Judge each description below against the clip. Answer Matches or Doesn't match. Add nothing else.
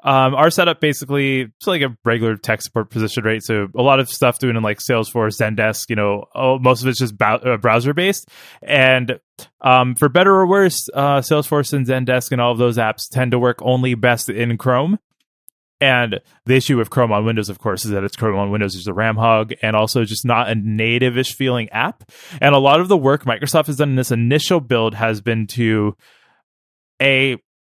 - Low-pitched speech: Matches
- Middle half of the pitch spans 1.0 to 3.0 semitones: Doesn't match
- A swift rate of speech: Matches